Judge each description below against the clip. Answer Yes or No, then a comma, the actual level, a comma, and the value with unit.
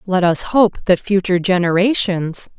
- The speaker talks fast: No, average, 140 wpm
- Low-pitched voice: No, medium, 185 Hz